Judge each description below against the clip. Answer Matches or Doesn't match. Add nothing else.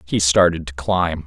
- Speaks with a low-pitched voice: Matches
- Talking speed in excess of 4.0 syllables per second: Matches